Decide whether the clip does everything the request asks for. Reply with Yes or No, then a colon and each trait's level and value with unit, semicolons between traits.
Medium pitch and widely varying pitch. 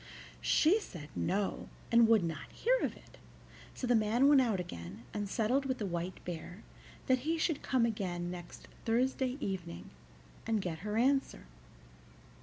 No: high, 220 Hz; wide, 6.6 semitones